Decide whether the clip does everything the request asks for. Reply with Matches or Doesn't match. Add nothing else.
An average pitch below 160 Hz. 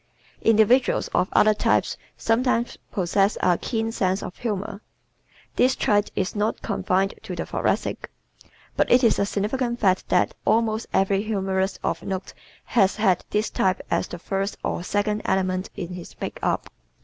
Doesn't match